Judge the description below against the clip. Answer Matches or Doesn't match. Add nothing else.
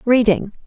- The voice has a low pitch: Doesn't match